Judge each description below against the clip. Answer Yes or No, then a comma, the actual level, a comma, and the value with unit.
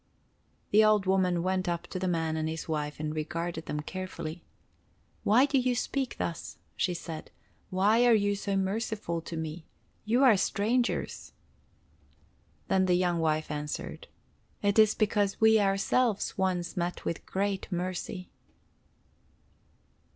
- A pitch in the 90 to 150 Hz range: No, medium, 185 Hz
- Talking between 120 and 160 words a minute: Yes, average, 140 wpm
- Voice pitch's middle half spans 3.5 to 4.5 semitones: Yes, average, 3.9 semitones